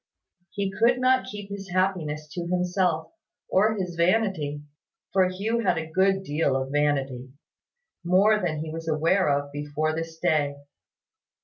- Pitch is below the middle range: No, medium, 175 Hz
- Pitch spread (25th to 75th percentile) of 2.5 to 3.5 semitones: No, average, 4.3 semitones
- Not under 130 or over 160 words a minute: Yes, average, 145 wpm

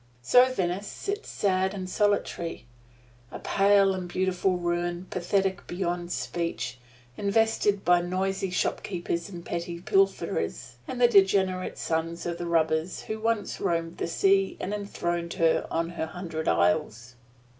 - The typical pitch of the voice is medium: Yes, medium, 180 Hz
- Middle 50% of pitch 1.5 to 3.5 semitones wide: Yes, narrow, 2.6 semitones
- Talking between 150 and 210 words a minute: No, slow, 135 wpm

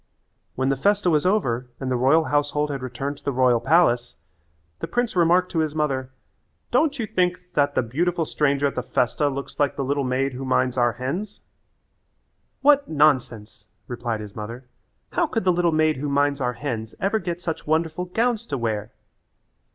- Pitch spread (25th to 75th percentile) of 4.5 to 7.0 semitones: Yes, average, 5.2 semitones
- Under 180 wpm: No, average, 185 wpm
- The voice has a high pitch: No, medium, 145 Hz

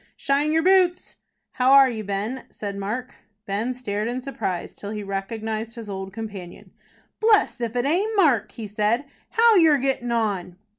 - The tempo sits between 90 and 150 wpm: No, average, 165 wpm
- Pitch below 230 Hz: No, high, 235 Hz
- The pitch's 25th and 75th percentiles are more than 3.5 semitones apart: Yes, average, 5.0 semitones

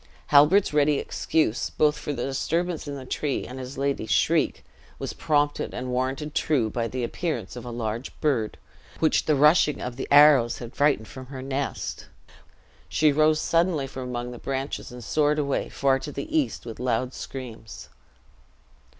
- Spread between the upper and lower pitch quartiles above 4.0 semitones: No, average, 3.3 semitones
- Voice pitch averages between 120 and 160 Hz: Yes, low, 135 Hz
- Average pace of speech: Yes, average, 170 wpm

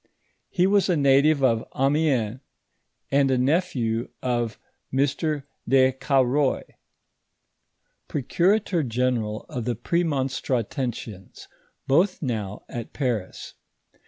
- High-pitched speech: No, low, 130 Hz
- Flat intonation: No, average, 3.8 semitones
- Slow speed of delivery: Yes, slow, 100 wpm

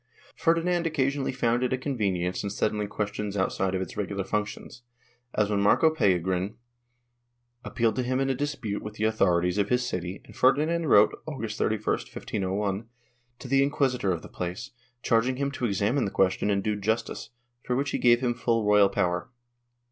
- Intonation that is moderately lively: Yes, average, 4.4 semitones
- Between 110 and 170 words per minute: No, average, 180 wpm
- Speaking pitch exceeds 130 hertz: No, low, 110 Hz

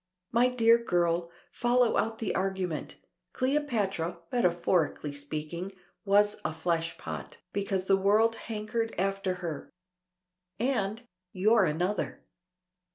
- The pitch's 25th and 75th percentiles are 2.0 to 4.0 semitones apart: No, average, 4.6 semitones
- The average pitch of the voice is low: No, high, 195 Hz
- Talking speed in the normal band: No, slow, 100 wpm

